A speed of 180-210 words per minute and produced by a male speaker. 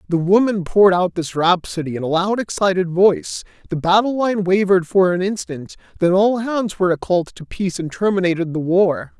Yes: average, 190 wpm; male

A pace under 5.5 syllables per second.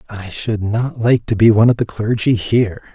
Yes: 5.3 syllables/s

